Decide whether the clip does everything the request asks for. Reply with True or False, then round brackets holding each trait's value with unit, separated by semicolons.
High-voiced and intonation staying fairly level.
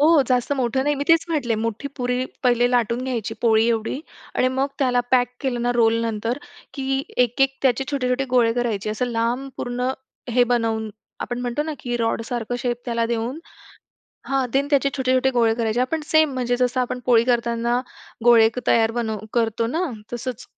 True (245 Hz; 2.2 semitones)